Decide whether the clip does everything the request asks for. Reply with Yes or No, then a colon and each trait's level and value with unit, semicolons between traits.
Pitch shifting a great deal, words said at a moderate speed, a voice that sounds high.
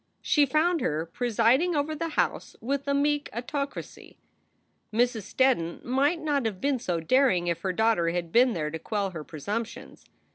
Yes: wide, 7.7 semitones; average, 175 wpm; high, 240 Hz